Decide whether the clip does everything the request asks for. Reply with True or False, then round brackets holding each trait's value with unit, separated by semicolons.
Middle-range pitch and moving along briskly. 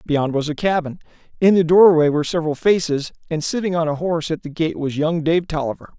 True (160 Hz; 220 wpm)